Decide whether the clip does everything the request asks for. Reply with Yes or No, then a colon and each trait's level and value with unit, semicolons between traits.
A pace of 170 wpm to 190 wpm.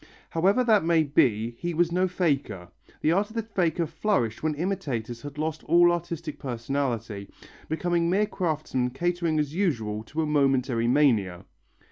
No: average, 155 wpm